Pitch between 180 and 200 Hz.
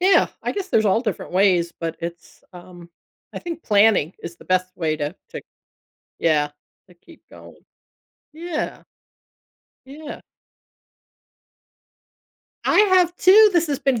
No: high, 210 Hz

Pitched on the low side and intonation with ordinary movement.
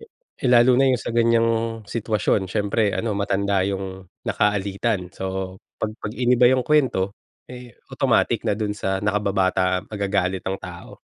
Yes: low, 105 Hz; average, 3.5 semitones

